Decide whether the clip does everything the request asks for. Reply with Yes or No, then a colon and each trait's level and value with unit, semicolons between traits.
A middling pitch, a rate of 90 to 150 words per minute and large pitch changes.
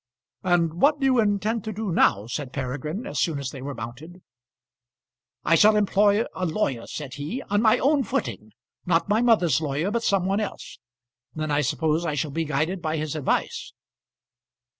No: medium, 165 Hz; average, 185 wpm; wide, 6.2 semitones